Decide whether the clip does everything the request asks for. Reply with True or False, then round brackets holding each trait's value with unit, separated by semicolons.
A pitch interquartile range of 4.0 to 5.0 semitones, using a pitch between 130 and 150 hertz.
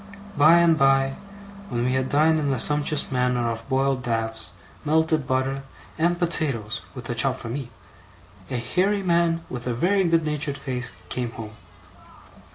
True (4.4 semitones; 135 Hz)